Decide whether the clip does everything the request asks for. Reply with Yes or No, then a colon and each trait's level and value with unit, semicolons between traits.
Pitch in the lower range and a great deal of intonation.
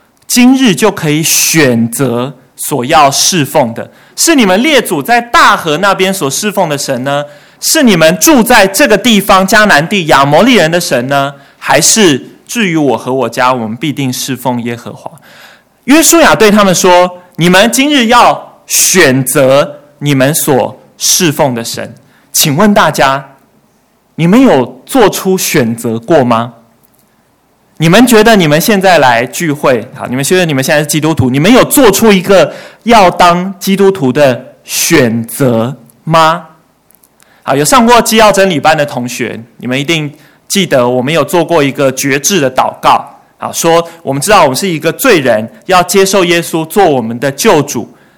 No: medium, 160 Hz; wide, 6.7 semitones